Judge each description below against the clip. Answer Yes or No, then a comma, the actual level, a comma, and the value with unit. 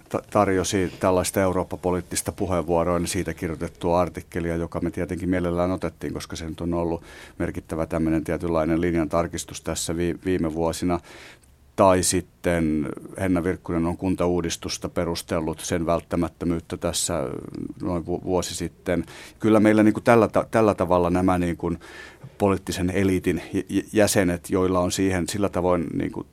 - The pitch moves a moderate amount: No, narrow, 1.6 semitones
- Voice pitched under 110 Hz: Yes, very low, 90 Hz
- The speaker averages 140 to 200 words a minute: No, average, 130 wpm